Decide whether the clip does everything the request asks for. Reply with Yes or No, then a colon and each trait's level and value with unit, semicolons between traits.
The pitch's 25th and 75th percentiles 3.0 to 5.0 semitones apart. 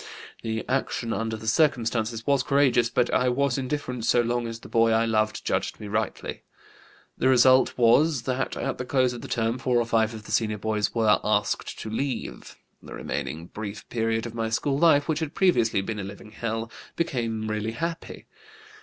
No: narrow, 2.6 semitones